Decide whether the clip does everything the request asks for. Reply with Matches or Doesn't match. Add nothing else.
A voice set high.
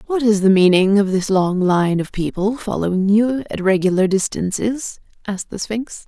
Matches